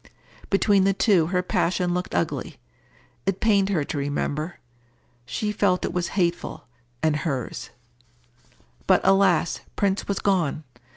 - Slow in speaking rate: Yes, slow, 130 wpm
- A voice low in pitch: No, medium, 180 Hz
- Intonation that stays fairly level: No, average, 3.6 semitones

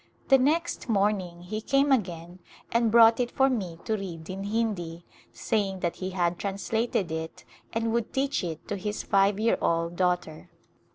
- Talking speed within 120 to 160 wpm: No, average, 170 wpm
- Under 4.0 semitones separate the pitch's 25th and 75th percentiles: No, average, 4.6 semitones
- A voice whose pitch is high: Yes, high, 200 Hz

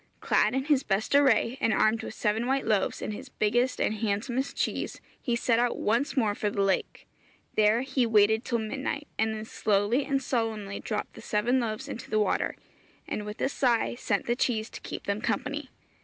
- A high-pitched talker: Yes, high, 225 Hz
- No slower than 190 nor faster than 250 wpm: Yes, average, 200 wpm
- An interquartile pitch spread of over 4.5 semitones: No, average, 3.3 semitones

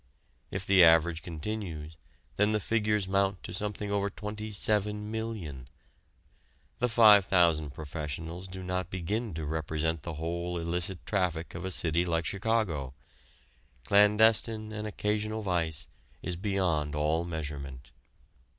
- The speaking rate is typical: No, slow, 125 wpm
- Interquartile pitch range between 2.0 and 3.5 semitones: No, average, 4.4 semitones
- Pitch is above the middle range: No, very low, 90 Hz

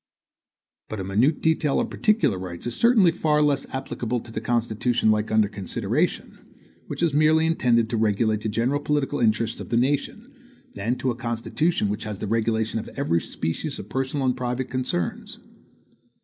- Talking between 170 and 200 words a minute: Yes, average, 175 wpm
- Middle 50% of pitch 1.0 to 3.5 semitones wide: No, average, 4.8 semitones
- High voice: No, low, 120 Hz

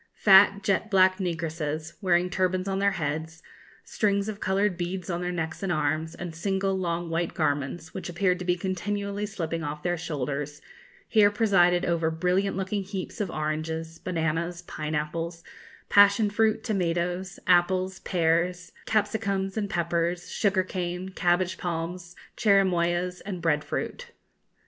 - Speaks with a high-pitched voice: No, medium, 180 Hz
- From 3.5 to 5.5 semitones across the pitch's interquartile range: No, narrow, 2.6 semitones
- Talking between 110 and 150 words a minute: Yes, average, 140 wpm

